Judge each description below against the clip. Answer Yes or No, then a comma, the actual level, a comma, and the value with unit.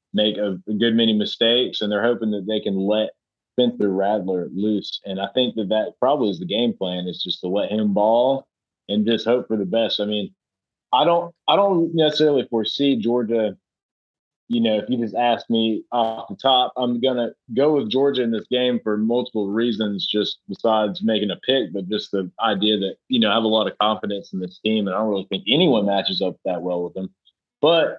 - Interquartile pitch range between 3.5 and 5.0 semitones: No, average, 2.7 semitones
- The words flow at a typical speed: No, fast, 215 wpm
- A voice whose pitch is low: Yes, low, 110 Hz